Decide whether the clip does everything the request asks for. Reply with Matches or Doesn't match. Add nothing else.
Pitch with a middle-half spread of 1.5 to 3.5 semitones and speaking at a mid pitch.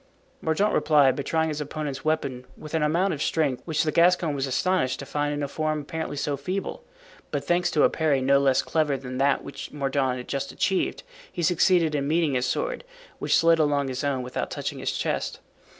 Matches